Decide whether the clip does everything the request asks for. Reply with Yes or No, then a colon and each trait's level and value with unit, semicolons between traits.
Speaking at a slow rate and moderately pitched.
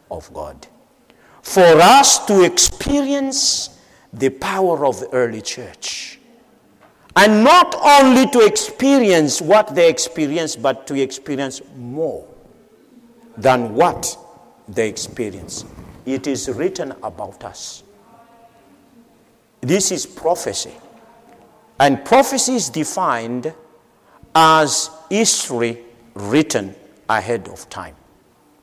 Yes: slow, 95 wpm; medium, 160 Hz